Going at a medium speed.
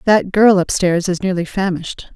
Yes: average, 195 wpm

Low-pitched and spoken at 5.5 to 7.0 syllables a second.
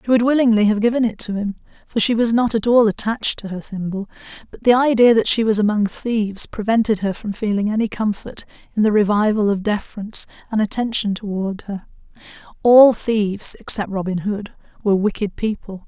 No: high, 215 Hz; 5.7 syllables/s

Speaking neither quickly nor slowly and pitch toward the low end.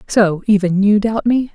No: average, 195 wpm; high, 205 Hz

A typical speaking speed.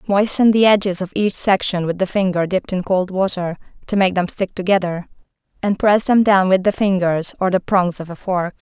No: fast, 215 wpm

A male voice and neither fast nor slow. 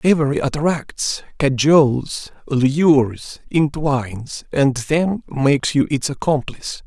No: male; slow, 95 wpm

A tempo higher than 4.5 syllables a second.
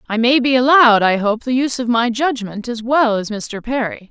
Yes: 5.3 syllables/s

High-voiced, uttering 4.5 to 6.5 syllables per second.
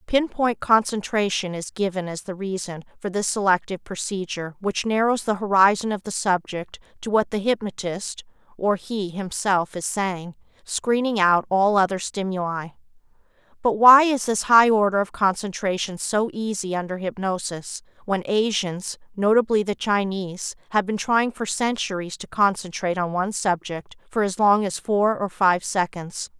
Yes: high, 200 Hz; 4.7 syllables/s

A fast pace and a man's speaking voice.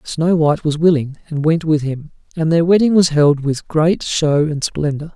Yes: fast, 210 wpm; male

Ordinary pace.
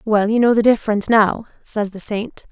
No: fast, 215 wpm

